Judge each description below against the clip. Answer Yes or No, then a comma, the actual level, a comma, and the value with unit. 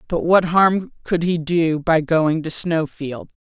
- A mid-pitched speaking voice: Yes, medium, 165 Hz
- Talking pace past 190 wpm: No, average, 175 wpm